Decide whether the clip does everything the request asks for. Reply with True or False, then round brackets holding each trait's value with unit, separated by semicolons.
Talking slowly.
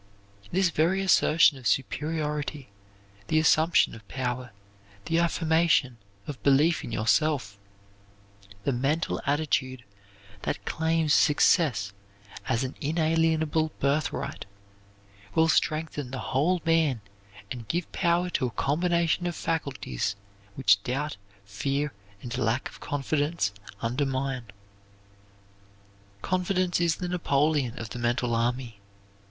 True (115 wpm)